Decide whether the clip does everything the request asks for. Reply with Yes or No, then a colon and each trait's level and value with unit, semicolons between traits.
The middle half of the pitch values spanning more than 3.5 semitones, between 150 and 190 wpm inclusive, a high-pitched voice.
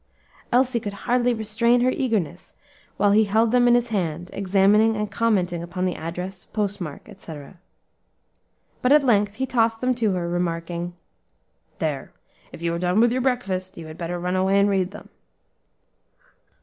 Yes: average, 4.6 semitones; average, 160 wpm; high, 200 Hz